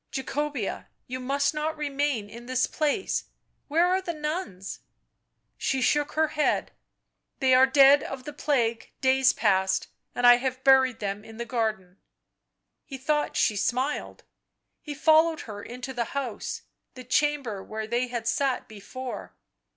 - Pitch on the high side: Yes, very high, 260 Hz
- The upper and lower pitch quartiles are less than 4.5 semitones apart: Yes, average, 4.0 semitones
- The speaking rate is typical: Yes, average, 160 wpm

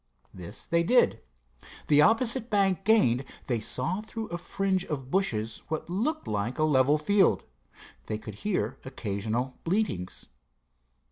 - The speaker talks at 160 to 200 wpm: No, slow, 135 wpm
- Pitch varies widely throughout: Yes, wide, 8.9 semitones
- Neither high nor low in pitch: Yes, medium, 155 Hz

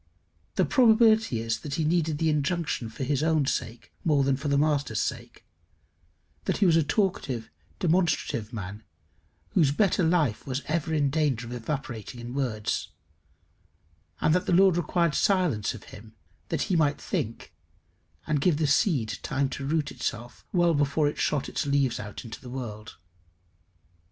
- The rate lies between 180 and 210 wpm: No, average, 165 wpm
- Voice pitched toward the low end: No, medium, 145 Hz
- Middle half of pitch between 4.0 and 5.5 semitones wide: Yes, average, 5.1 semitones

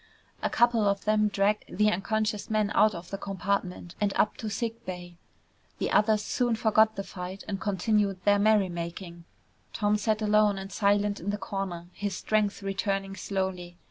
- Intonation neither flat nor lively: No, narrow, 1.8 semitones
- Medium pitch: No, high, 200 Hz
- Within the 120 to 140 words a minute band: No, average, 170 wpm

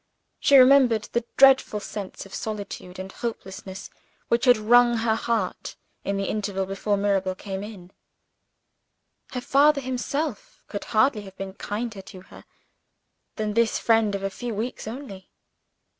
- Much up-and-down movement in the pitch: No, average, 3.7 semitones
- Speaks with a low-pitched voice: No, high, 215 Hz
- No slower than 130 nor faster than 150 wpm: Yes, average, 145 wpm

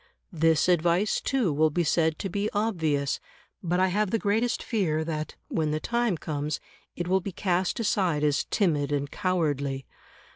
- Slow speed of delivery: No, average, 170 wpm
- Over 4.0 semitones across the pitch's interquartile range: Yes, average, 4.5 semitones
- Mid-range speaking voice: Yes, medium, 175 Hz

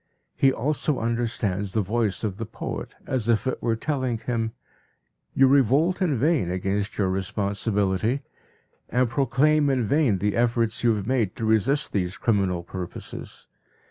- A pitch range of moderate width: Yes, average, 4.6 semitones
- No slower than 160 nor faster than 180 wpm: No, average, 150 wpm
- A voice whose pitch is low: Yes, low, 115 Hz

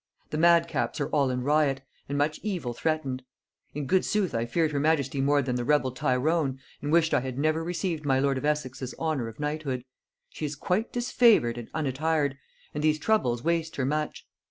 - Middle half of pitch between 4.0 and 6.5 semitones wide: No, average, 3.4 semitones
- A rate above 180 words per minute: Yes, average, 195 wpm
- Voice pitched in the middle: Yes, medium, 150 Hz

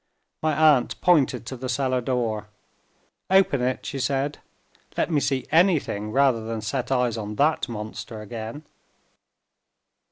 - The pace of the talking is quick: No, slow, 135 wpm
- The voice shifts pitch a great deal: No, average, 3.9 semitones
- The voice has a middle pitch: No, low, 130 Hz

